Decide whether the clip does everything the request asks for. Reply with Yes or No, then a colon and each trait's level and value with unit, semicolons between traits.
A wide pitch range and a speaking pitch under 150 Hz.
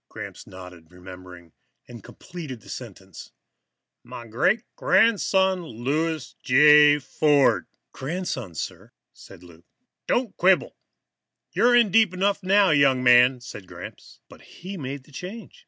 Yes: wide, 8.6 semitones; medium, 140 Hz